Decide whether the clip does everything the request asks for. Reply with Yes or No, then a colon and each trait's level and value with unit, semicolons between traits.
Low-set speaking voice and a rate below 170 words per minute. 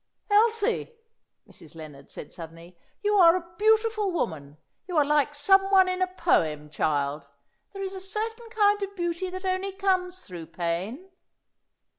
No: very high, 365 Hz; average, 155 wpm